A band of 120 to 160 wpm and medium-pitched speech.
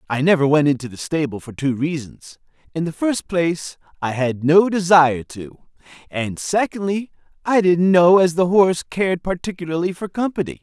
No: average, 170 wpm; medium, 165 Hz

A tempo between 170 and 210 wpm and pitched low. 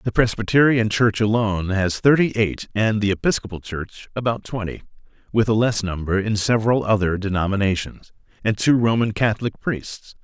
No: average, 150 wpm; low, 105 Hz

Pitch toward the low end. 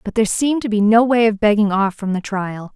No: high, 215 Hz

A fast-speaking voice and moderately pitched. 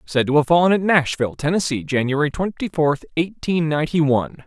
No: average, 175 wpm; medium, 155 Hz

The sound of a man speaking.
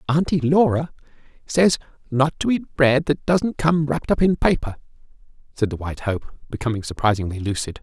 Yes: male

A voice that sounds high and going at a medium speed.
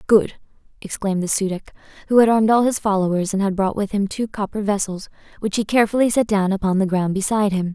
No: high, 205 Hz; fast, 225 wpm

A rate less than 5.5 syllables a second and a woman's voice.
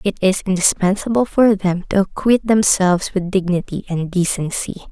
Yes: 5.1 syllables/s; female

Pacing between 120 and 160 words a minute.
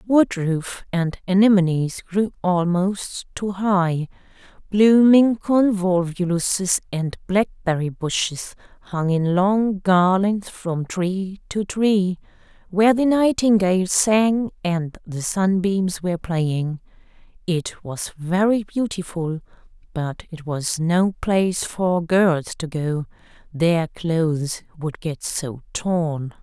No: slow, 110 wpm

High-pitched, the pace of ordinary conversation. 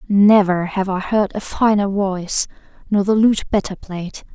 Yes: high, 200 Hz; average, 165 wpm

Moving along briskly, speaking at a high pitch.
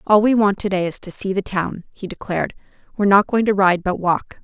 Yes: fast, 255 wpm; high, 195 Hz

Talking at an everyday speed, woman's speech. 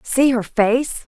Yes: average, 150 wpm; female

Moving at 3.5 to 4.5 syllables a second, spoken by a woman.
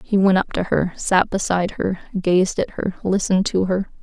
No: 5.1 syllables/s; female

